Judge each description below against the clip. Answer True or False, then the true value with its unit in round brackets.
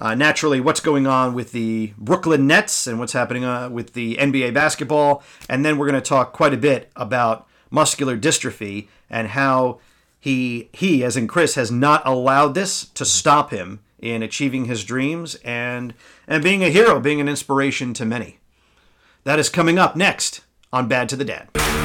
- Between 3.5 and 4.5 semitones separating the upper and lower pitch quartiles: True (4.0 semitones)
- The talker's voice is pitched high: False (130 Hz)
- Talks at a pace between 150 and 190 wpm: True (185 wpm)